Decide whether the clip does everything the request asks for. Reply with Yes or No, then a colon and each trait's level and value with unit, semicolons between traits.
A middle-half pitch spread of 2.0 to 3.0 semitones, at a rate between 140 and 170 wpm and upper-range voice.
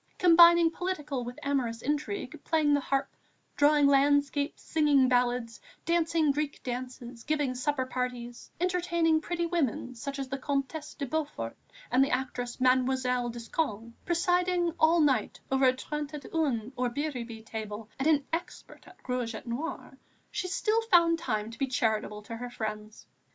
No: average, 4.5 semitones; average, 155 wpm; very high, 275 Hz